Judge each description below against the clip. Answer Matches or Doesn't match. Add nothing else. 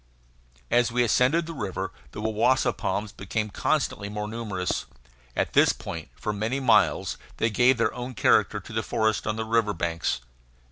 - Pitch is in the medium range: Doesn't match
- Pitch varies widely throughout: Doesn't match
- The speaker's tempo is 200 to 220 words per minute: Doesn't match